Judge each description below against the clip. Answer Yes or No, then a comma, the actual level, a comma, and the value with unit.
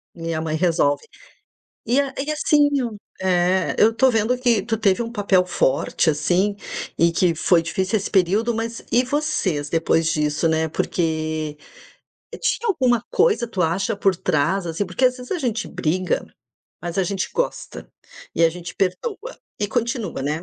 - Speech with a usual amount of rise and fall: No, wide, 6.1 semitones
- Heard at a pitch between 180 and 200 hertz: Yes, high, 190 Hz